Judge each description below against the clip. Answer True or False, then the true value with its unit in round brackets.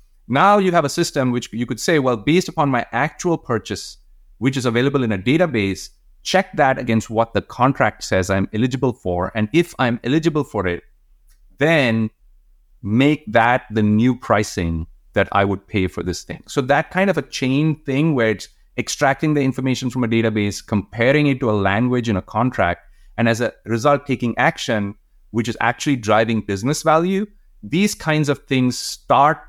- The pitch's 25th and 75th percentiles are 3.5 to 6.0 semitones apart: True (5.2 semitones)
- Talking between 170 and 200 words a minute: True (185 wpm)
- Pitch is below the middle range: True (120 Hz)